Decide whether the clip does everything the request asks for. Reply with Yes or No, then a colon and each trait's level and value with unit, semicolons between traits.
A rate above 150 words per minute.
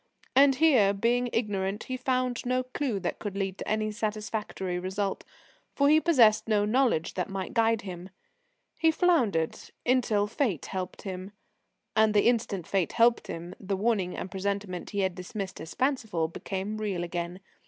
Yes: average, 165 wpm